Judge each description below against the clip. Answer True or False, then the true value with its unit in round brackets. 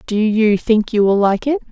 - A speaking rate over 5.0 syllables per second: False (4.7 syllables/s)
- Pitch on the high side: True (220 Hz)